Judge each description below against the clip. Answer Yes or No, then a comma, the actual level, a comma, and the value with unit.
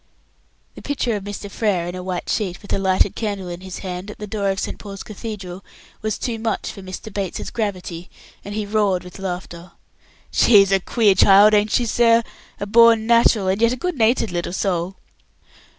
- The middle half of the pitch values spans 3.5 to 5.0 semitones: No, average, 2.7 semitones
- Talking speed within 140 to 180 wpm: No, average, 195 wpm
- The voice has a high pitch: Yes, high, 200 Hz